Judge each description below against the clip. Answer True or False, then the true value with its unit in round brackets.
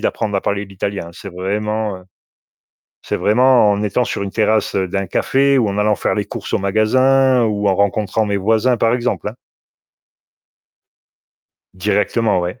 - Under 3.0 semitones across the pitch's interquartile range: True (2.4 semitones)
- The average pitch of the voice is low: True (105 Hz)